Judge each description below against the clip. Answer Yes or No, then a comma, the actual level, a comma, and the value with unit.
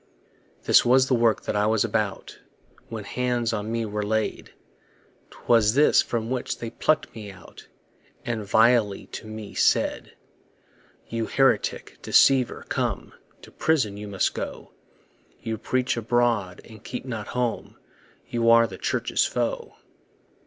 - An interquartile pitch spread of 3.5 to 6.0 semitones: No, narrow, 2.4 semitones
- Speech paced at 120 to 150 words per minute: Yes, average, 140 wpm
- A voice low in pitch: Yes, low, 115 Hz